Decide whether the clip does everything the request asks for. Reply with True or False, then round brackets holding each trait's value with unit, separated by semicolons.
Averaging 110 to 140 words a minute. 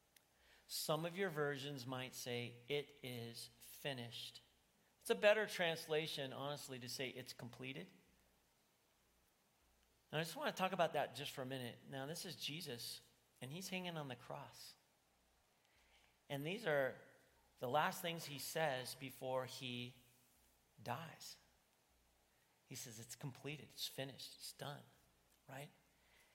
True (135 wpm)